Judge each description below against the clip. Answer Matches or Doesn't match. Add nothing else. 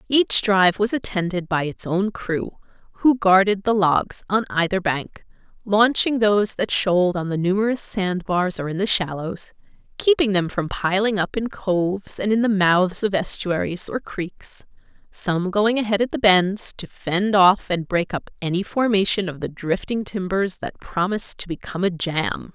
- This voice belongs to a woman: Matches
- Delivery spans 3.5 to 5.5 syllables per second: Matches